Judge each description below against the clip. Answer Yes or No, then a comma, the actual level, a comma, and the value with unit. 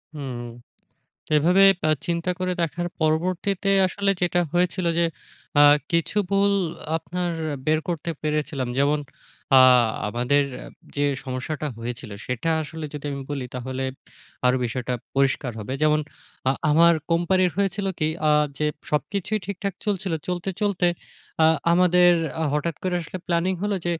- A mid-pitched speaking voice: Yes, medium, 170 Hz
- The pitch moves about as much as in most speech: Yes, average, 4.1 semitones